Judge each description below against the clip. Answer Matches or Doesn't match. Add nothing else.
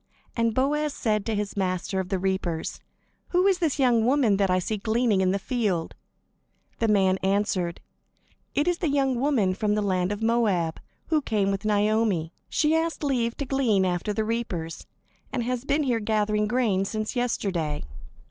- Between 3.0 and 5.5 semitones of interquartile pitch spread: Matches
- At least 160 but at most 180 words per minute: Matches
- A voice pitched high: Matches